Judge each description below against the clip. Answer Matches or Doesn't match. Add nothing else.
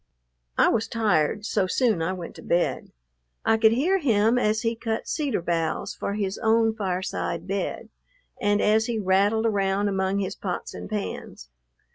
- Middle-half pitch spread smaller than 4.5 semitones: Matches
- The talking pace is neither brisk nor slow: Matches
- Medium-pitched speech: Doesn't match